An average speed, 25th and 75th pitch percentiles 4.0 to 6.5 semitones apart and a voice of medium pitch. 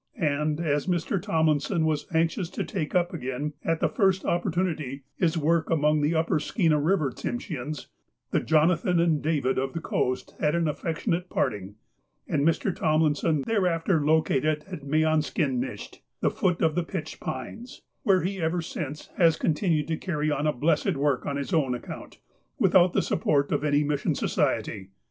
No: average, 165 wpm; narrow, 2.6 semitones; medium, 155 Hz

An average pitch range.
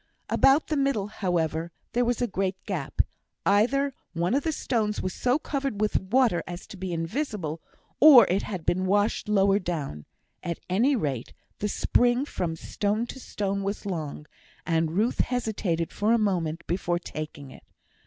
No: wide, 5.8 semitones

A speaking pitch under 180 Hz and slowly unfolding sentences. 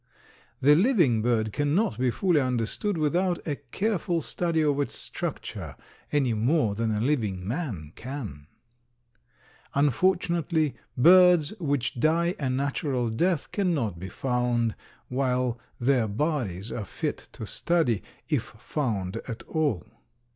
Yes: low, 135 Hz; slow, 125 wpm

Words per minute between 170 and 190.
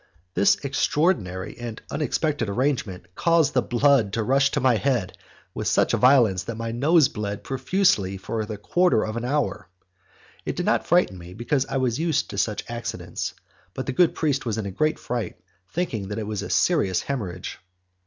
Yes: average, 185 wpm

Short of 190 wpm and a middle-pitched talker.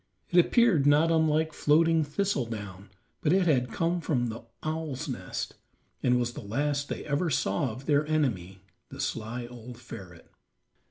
Yes: average, 160 wpm; medium, 145 Hz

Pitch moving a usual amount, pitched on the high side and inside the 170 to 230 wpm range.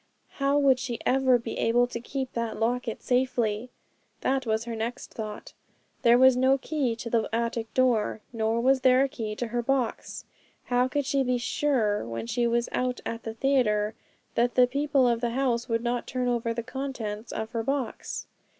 No: narrow, 2.3 semitones; high, 240 Hz; average, 190 wpm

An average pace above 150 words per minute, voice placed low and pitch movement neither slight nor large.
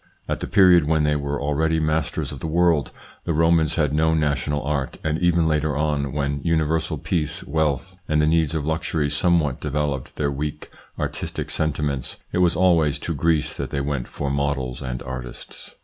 No: average, 180 wpm; very low, 75 Hz; narrow, 2.1 semitones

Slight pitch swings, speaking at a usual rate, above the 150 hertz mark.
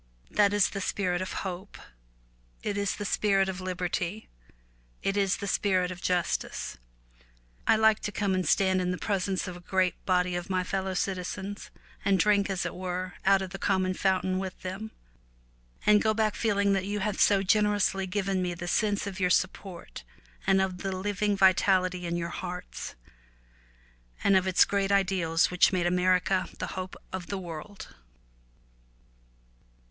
Yes: narrow, 1.6 semitones; average, 165 wpm; high, 190 Hz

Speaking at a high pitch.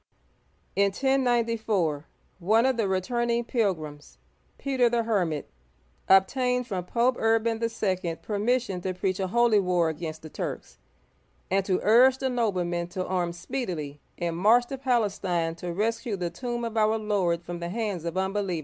Yes: high, 200 Hz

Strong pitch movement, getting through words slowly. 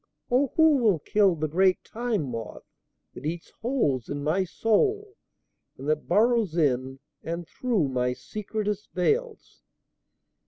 Yes: wide, 7.9 semitones; slow, 130 wpm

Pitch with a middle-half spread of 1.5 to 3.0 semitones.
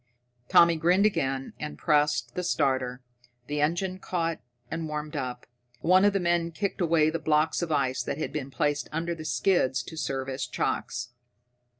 No: average, 3.9 semitones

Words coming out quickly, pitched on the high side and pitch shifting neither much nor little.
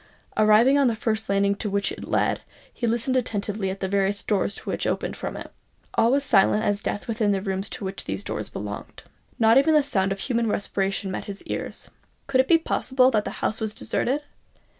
Yes: fast, 210 wpm; high, 215 Hz; average, 3.7 semitones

